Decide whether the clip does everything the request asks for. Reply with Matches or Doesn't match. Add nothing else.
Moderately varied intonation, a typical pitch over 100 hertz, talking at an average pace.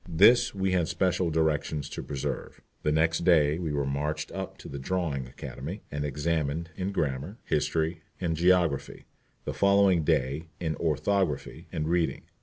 Doesn't match